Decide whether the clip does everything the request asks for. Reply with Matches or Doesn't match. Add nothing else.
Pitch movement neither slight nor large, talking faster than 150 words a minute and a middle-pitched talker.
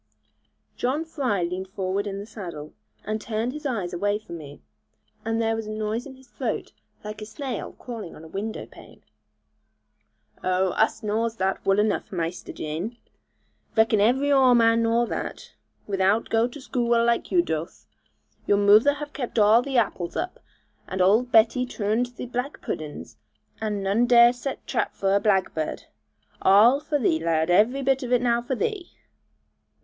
Doesn't match